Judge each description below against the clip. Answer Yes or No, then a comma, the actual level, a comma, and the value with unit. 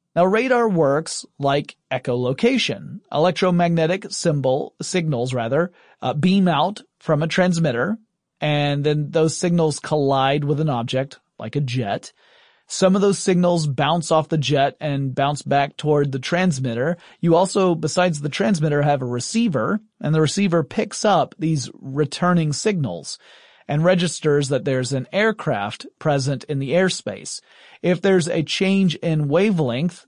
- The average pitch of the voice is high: No, medium, 160 Hz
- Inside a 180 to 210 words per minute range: No, average, 145 wpm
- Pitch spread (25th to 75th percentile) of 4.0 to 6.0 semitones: Yes, average, 4.4 semitones